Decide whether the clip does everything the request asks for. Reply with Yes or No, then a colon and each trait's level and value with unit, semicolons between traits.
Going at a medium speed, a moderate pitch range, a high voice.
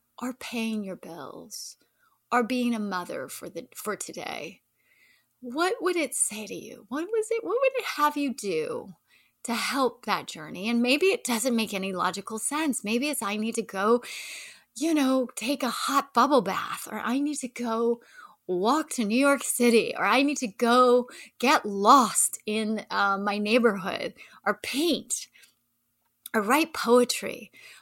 Yes: average, 170 wpm; average, 4.6 semitones; high, 245 Hz